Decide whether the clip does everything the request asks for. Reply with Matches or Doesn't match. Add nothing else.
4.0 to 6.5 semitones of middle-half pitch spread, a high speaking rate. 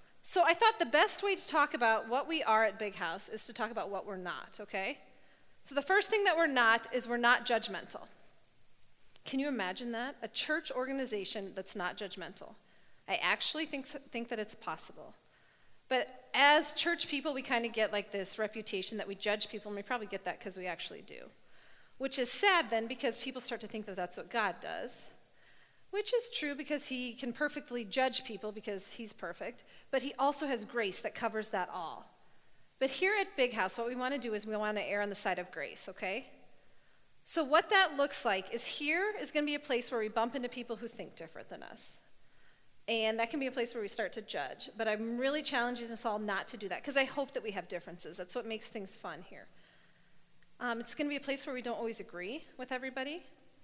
Matches